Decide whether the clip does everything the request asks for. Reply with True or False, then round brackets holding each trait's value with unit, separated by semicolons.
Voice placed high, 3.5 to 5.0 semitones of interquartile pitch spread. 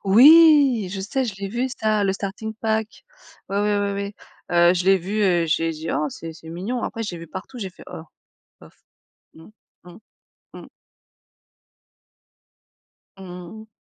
True (195 Hz; 3.8 semitones)